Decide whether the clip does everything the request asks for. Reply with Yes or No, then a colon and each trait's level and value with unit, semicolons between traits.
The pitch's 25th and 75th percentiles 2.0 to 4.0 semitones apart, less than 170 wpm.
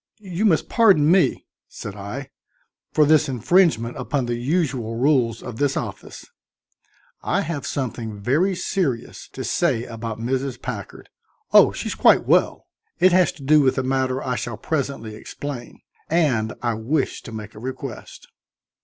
No: average, 5.0 semitones; average, 155 wpm